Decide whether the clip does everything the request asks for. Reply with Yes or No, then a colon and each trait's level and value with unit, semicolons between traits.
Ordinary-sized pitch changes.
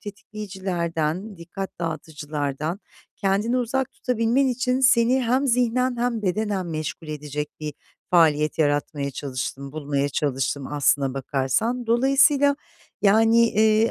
No: wide, 7.9 semitones